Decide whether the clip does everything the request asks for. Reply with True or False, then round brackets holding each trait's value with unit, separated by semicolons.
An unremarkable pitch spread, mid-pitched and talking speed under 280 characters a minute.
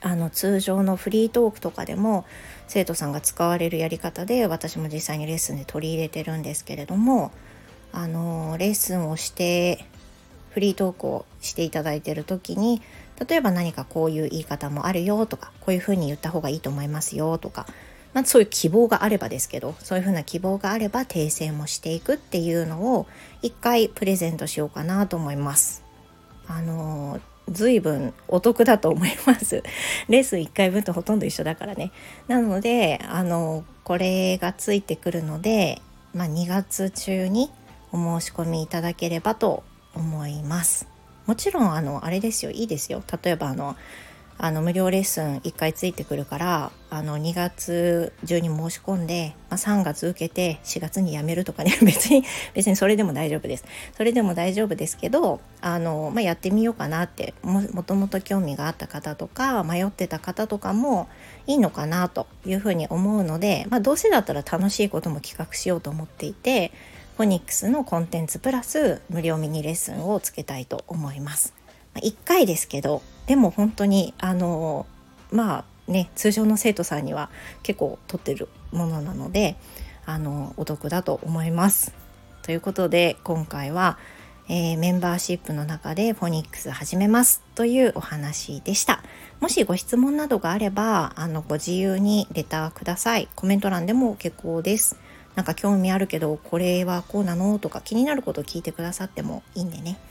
False (4.3 semitones; 175 Hz; 355 characters per minute)